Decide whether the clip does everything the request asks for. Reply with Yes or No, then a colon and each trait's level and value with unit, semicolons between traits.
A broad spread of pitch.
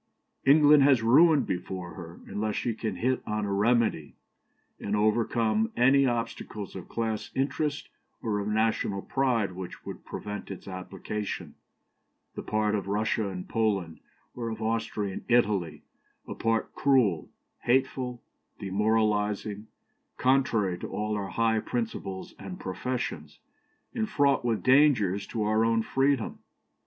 No: average, 3.5 semitones